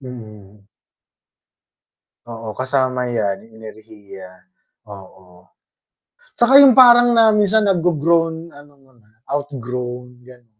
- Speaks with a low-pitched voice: Yes, low, 125 Hz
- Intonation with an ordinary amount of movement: No, wide, 7.3 semitones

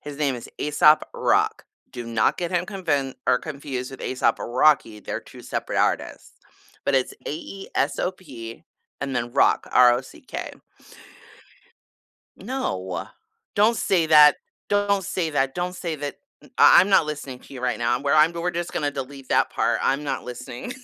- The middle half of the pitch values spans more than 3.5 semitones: Yes, average, 5.2 semitones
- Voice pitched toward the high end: No, medium, 145 Hz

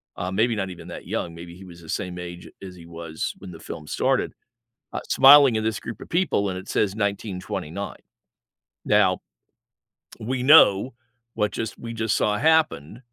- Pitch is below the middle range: Yes, low, 100 Hz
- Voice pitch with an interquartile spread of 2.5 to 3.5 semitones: No, average, 4.5 semitones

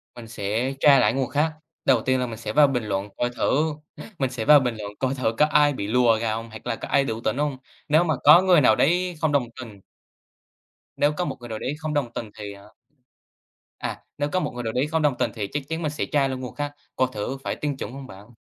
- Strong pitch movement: No, average, 4.5 semitones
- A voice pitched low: Yes, low, 130 Hz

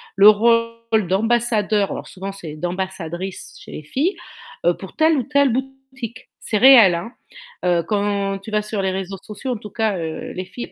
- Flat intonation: No, average, 3.8 semitones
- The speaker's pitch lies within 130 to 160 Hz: No, high, 210 Hz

